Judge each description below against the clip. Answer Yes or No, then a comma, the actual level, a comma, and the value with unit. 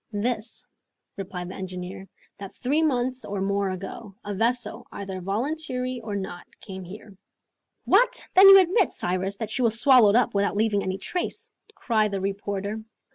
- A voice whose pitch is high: Yes, high, 205 Hz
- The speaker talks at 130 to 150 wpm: No, average, 160 wpm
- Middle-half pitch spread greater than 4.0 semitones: Yes, average, 4.4 semitones